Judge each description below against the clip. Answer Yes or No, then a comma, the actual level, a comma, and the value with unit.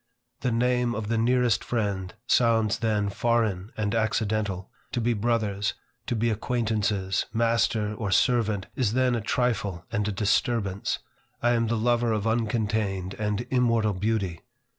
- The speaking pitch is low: Yes, low, 110 Hz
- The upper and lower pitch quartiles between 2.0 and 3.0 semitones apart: Yes, narrow, 2.5 semitones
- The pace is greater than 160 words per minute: No, average, 145 wpm